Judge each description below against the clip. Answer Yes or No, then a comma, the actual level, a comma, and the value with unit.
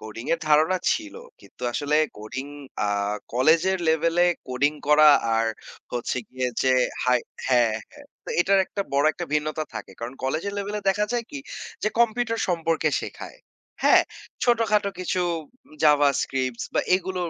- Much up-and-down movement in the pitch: Yes, wide, 7.3 semitones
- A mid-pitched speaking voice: Yes, medium, 155 Hz